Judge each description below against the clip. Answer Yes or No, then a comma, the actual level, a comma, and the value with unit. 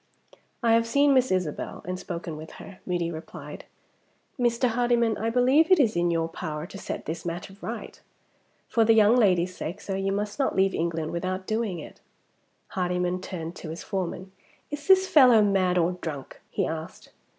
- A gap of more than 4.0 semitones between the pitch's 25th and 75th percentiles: Yes, average, 5.1 semitones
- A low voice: No, high, 190 Hz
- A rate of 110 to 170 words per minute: No, average, 180 wpm